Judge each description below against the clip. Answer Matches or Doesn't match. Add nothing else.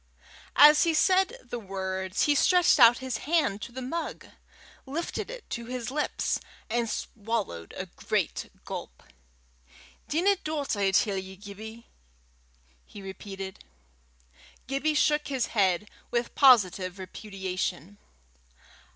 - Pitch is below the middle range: Doesn't match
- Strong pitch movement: Matches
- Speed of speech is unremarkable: Doesn't match